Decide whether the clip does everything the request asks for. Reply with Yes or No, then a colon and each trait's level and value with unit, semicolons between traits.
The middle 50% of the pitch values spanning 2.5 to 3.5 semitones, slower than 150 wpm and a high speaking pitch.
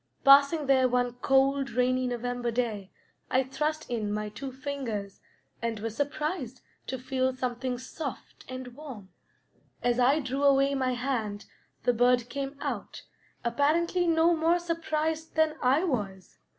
Yes: average, 2.8 semitones; average, 140 wpm; very high, 260 Hz